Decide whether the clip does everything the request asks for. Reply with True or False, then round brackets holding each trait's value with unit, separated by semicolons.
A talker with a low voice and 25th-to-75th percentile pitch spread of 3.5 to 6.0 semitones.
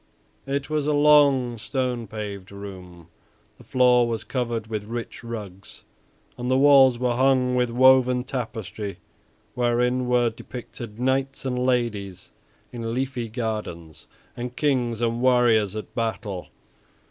False (120 Hz; 2.6 semitones)